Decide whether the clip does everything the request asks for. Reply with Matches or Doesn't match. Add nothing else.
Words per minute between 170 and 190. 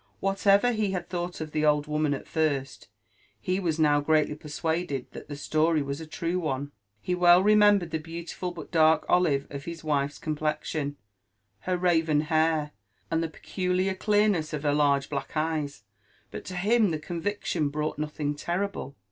Matches